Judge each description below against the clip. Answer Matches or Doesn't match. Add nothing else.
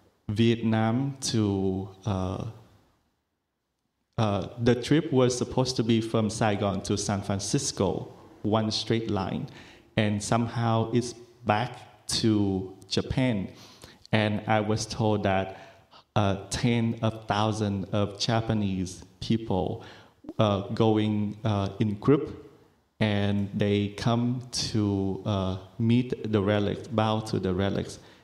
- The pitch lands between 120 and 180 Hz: Doesn't match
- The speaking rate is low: Matches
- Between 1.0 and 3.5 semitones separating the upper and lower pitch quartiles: Matches